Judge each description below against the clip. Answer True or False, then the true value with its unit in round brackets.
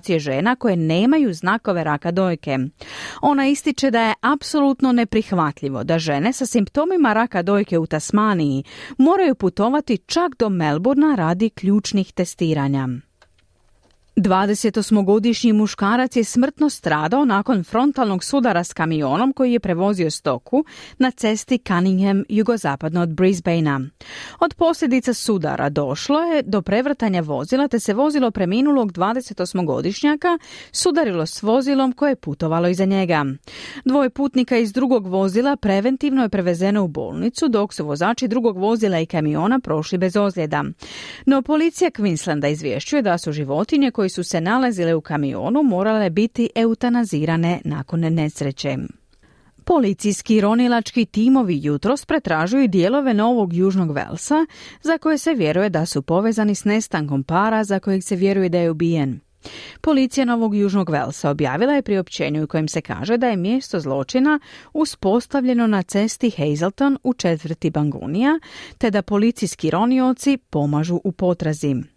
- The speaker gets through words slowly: False (135 wpm)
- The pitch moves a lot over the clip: True (7.3 semitones)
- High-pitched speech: True (205 Hz)